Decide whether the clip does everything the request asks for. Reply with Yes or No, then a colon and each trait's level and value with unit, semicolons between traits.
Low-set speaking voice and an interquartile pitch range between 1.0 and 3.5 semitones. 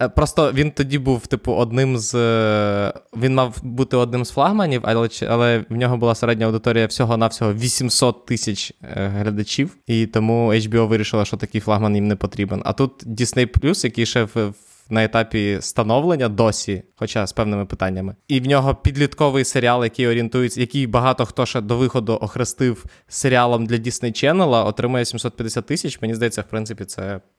Yes: low, 115 Hz; average, 2.7 semitones